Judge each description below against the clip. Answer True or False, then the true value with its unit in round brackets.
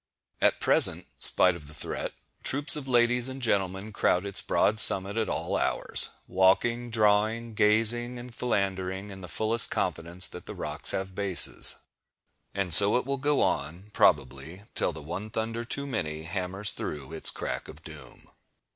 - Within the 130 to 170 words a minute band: True (160 wpm)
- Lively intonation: False (4.3 semitones)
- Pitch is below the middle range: True (100 Hz)